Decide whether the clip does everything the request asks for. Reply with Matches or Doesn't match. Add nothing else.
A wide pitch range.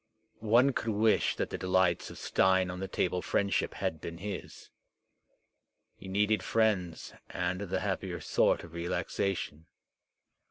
Doesn't match